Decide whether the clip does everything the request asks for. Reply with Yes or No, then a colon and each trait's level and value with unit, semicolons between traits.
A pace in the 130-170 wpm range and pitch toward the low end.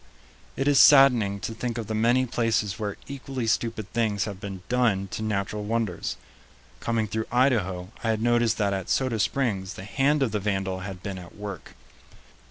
No: average, 180 wpm; low, 110 Hz